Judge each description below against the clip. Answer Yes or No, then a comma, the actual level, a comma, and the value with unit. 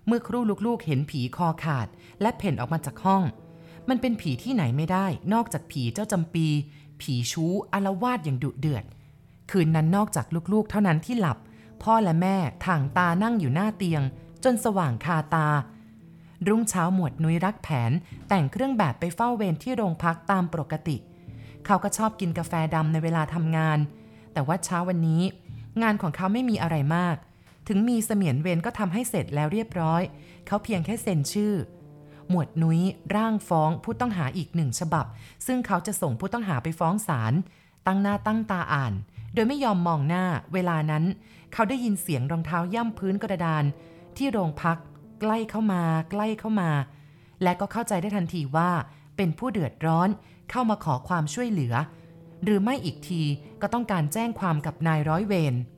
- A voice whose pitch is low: No, medium, 170 Hz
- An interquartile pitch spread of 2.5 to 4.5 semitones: No, average, 4.9 semitones